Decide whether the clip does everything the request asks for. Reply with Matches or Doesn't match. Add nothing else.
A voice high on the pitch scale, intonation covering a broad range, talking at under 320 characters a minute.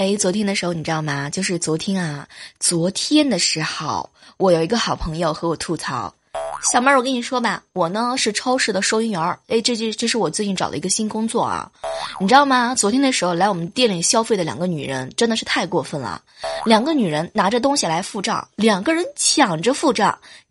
Doesn't match